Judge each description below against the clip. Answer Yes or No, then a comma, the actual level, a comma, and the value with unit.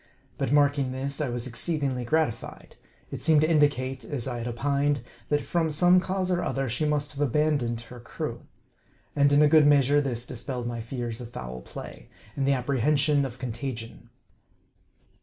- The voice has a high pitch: No, medium, 140 Hz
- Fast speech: No, average, 180 wpm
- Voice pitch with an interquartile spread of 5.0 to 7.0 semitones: No, average, 3.3 semitones